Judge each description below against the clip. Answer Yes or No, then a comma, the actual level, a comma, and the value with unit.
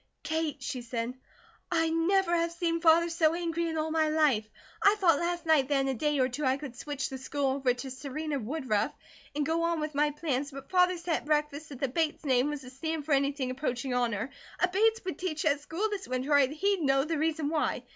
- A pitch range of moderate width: Yes, average, 3.5 semitones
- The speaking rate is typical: No, fast, 230 wpm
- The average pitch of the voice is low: No, very high, 300 Hz